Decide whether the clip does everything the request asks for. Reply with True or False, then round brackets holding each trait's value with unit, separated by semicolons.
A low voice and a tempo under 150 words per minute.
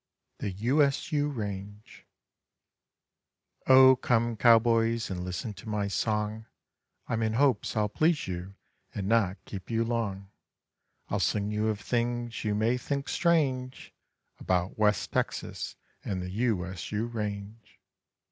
True (110 Hz; 140 wpm)